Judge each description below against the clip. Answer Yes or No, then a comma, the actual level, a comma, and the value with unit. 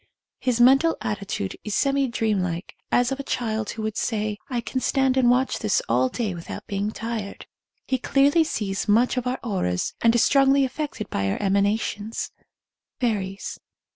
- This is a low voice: No, high, 225 Hz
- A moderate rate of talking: Yes, average, 175 wpm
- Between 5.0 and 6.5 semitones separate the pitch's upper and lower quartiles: No, average, 4.3 semitones